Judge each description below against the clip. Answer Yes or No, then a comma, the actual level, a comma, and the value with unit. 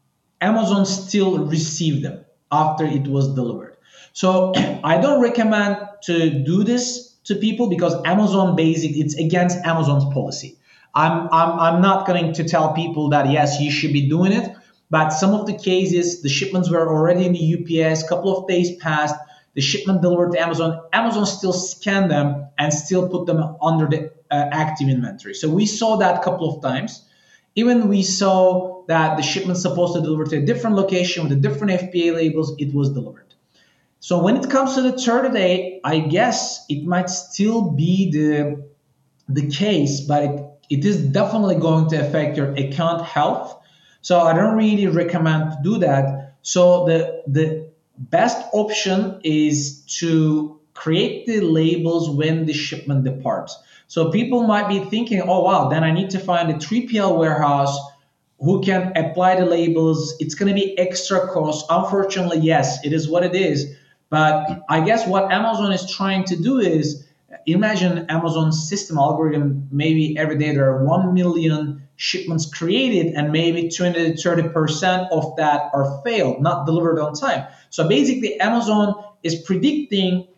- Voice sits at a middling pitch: Yes, medium, 165 Hz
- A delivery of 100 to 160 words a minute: No, average, 170 wpm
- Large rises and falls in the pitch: No, average, 3.7 semitones